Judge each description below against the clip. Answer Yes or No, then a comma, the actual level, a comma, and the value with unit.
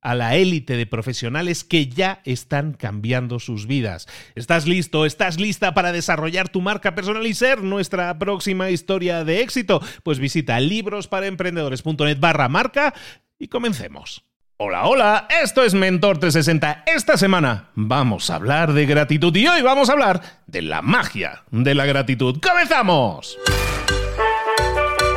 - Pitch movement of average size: No, wide, 6.7 semitones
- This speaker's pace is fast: No, average, 140 wpm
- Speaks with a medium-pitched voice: Yes, medium, 175 Hz